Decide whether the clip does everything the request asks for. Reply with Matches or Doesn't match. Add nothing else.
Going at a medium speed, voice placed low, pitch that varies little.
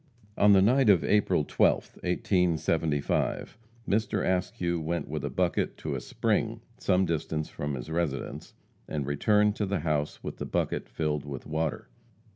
Doesn't match